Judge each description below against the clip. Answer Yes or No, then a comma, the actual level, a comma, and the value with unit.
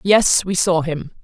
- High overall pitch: No, medium, 170 Hz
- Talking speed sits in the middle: Yes, average, 195 wpm